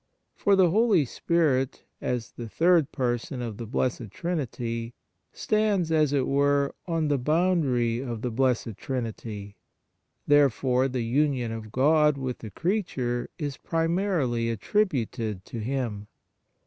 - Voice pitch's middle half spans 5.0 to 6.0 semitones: Yes, wide, 5.4 semitones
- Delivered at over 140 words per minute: No, slow, 135 wpm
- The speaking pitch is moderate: No, low, 130 Hz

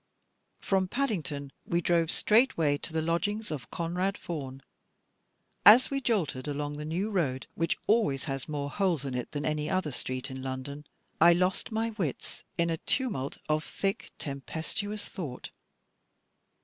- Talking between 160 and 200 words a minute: No, average, 150 wpm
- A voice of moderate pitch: Yes, medium, 165 Hz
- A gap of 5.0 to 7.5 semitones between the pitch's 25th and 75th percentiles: Yes, wide, 5.5 semitones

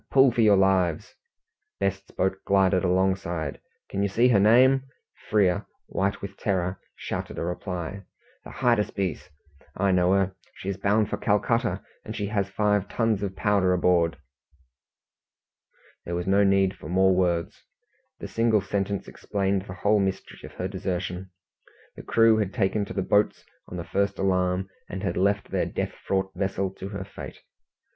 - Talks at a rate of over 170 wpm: No, average, 165 wpm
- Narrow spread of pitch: Yes, narrow, 1.7 semitones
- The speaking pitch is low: Yes, very low, 95 Hz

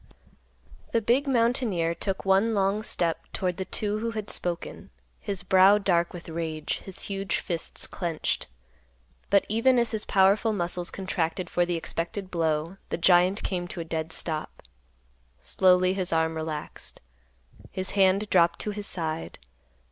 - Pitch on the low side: No, medium, 185 Hz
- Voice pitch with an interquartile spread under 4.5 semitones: Yes, average, 3.2 semitones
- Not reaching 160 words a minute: Yes, average, 150 wpm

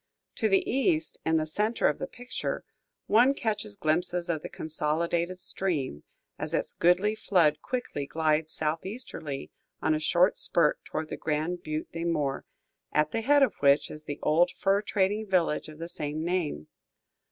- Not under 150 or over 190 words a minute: Yes, average, 165 wpm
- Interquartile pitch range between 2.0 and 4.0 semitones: No, average, 4.8 semitones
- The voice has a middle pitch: Yes, medium, 170 Hz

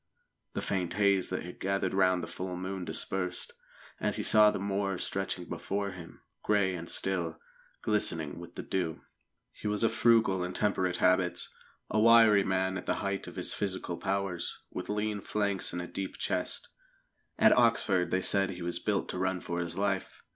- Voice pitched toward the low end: Yes, very low, 95 Hz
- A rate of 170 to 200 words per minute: Yes, average, 185 wpm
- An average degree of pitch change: No, narrow, 2.0 semitones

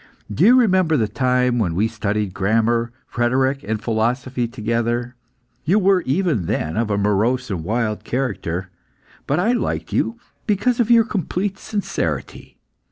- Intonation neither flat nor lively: No, wide, 8.7 semitones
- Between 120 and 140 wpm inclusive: No, average, 150 wpm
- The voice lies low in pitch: Yes, low, 120 Hz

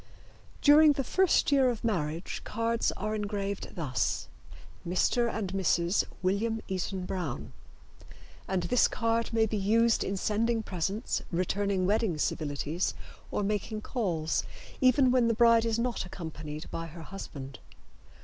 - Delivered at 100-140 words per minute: Yes, slow, 135 wpm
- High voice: Yes, high, 205 Hz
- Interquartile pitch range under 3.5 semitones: No, average, 4.7 semitones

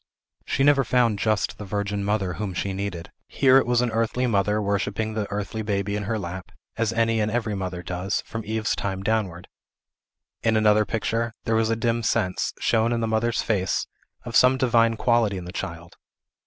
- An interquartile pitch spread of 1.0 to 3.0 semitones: Yes, narrow, 2.5 semitones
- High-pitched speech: No, low, 110 Hz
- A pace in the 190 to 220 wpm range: Yes, average, 195 wpm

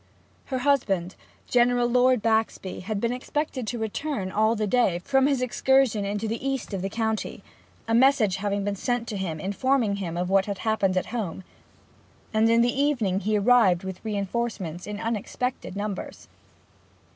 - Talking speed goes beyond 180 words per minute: No, average, 170 wpm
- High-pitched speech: Yes, high, 220 Hz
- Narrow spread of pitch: No, average, 4.0 semitones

